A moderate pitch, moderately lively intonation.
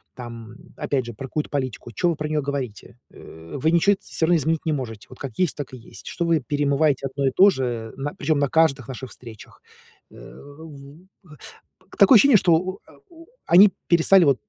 Yes: medium, 145 Hz; average, 4.2 semitones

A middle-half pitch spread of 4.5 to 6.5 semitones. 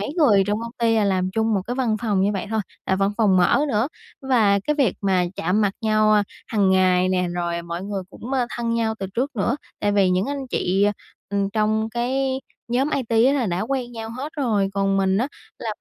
No: average, 3.7 semitones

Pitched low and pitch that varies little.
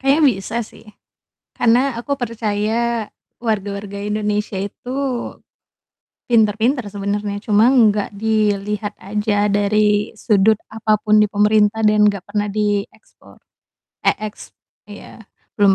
No: high, 210 Hz; narrow, 1.4 semitones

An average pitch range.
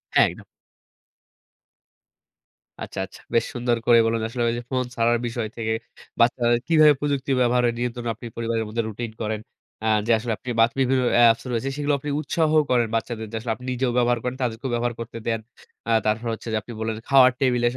No: narrow, 1.7 semitones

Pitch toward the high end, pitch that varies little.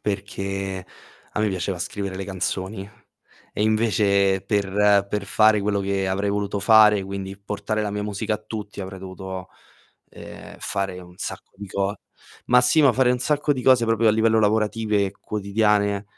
No: low, 100 Hz; narrow, 1.8 semitones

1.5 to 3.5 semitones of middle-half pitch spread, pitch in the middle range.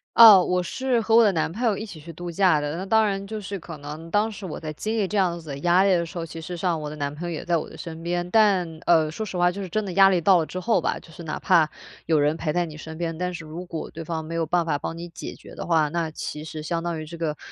Yes: average, 3.2 semitones; medium, 170 Hz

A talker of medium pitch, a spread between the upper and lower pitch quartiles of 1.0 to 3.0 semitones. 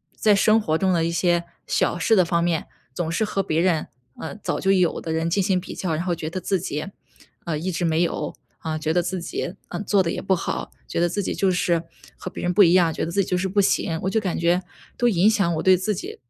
Yes: medium, 180 Hz; narrow, 2.4 semitones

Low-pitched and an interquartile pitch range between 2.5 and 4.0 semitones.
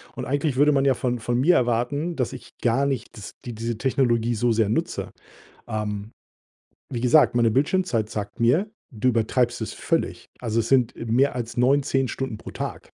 Yes: low, 120 Hz; average, 2.8 semitones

